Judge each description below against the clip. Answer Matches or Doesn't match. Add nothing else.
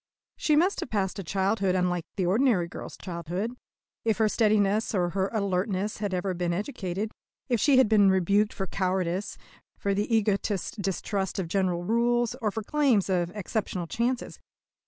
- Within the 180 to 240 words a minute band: Doesn't match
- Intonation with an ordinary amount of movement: Matches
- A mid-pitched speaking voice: Doesn't match